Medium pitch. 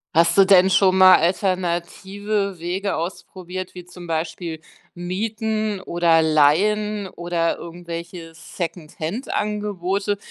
Yes: medium, 180 Hz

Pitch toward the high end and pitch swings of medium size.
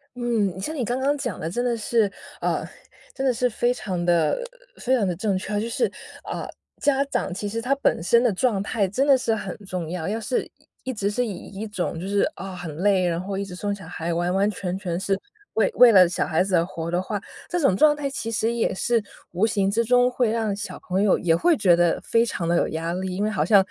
Yes: high, 205 Hz; average, 4.6 semitones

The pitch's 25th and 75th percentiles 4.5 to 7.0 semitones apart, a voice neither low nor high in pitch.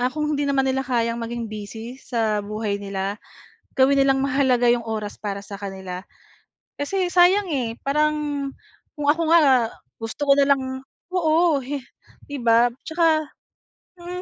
No: average, 5.0 semitones; very high, 260 Hz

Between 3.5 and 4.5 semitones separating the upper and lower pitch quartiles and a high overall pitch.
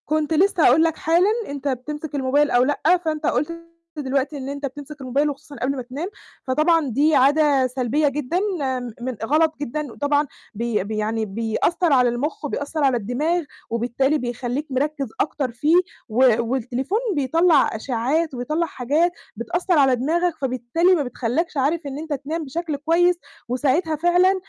Yes: average, 3.8 semitones; very high, 285 Hz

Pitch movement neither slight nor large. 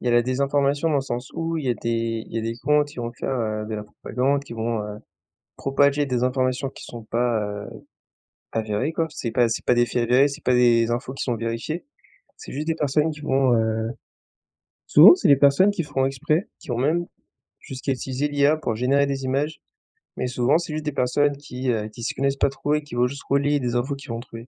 Yes: average, 3.3 semitones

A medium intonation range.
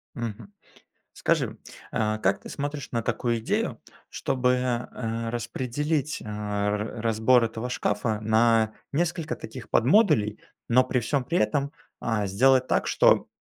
Yes: average, 3.3 semitones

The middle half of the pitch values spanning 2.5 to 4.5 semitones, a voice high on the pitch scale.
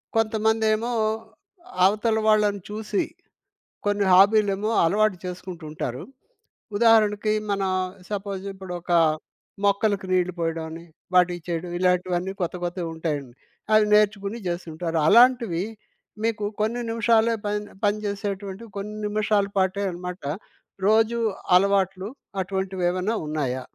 Yes: average, 2.9 semitones; high, 200 Hz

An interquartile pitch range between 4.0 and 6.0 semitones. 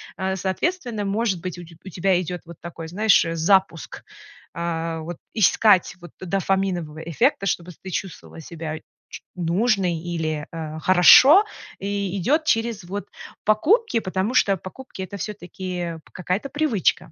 No: average, 3.4 semitones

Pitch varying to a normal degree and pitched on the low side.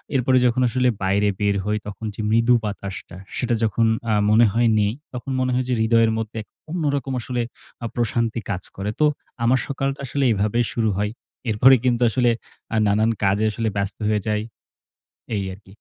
Yes: average, 3.1 semitones; low, 115 Hz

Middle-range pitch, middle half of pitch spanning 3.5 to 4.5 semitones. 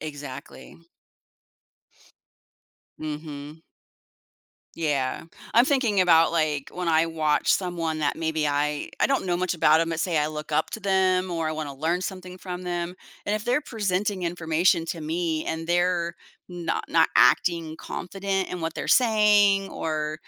No: medium, 170 Hz; average, 2.8 semitones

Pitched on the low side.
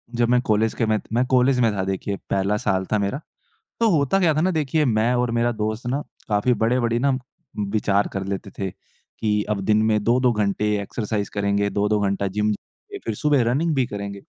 Yes: low, 110 Hz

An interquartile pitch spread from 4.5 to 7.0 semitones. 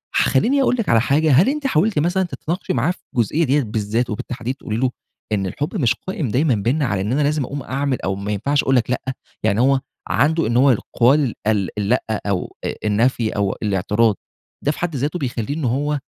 Yes: average, 5.3 semitones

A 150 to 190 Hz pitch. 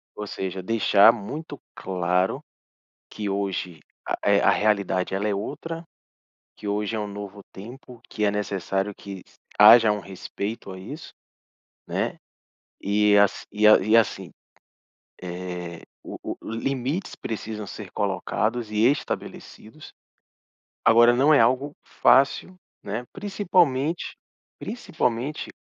No: low, 105 Hz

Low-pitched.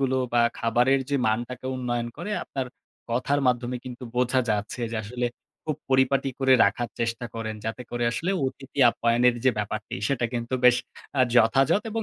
Yes: low, 125 Hz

